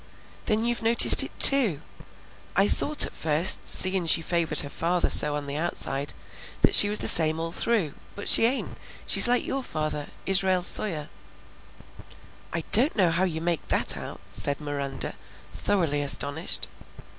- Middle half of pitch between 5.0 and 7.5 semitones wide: Yes, average, 5.3 semitones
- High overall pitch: No, medium, 170 Hz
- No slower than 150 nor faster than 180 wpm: Yes, average, 160 wpm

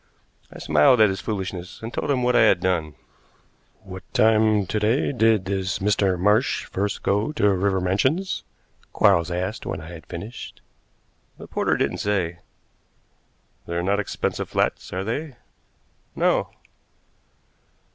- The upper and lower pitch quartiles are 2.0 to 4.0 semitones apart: Yes, average, 3.2 semitones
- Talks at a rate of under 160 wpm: Yes, average, 140 wpm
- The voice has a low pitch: Yes, low, 100 Hz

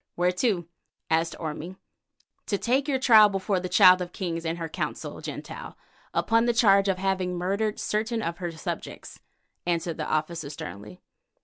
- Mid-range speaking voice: Yes, medium, 180 Hz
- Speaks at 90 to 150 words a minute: No, average, 165 wpm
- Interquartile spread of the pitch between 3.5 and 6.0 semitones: Yes, average, 3.9 semitones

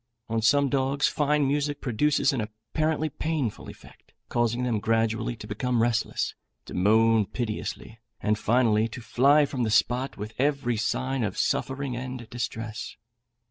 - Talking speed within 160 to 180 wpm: No, average, 145 wpm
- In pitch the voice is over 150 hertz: No, low, 120 Hz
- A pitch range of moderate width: Yes, average, 3.7 semitones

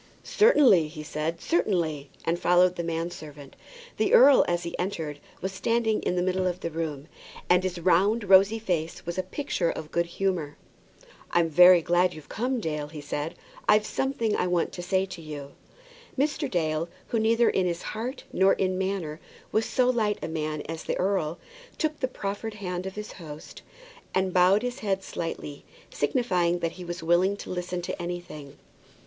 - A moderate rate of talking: Yes, average, 180 wpm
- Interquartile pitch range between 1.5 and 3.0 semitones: No, average, 3.5 semitones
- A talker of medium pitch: Yes, medium, 180 Hz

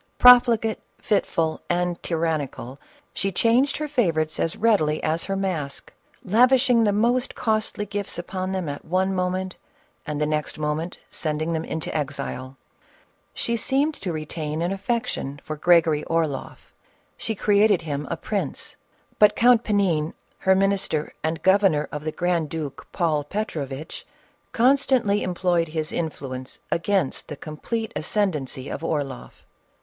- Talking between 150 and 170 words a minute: No, average, 140 wpm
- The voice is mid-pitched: Yes, medium, 175 Hz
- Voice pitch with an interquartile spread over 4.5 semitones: Yes, average, 5.2 semitones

